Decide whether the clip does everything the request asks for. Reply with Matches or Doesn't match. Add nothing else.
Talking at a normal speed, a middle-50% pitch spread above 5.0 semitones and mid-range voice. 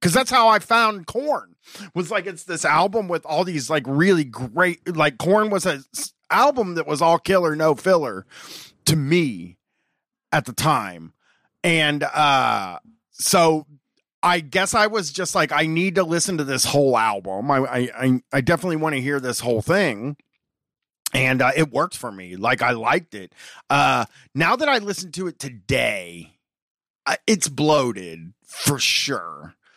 Matches